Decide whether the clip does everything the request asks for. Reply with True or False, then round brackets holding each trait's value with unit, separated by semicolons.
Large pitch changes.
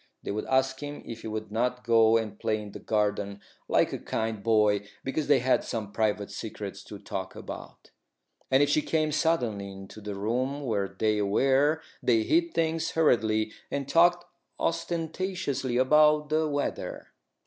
True (5.9 semitones)